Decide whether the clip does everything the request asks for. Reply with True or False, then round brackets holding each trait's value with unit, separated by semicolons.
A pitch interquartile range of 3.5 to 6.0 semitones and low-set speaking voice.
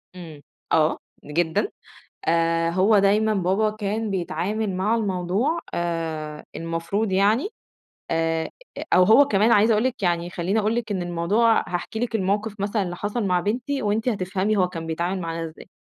False (4.0 semitones; 195 Hz)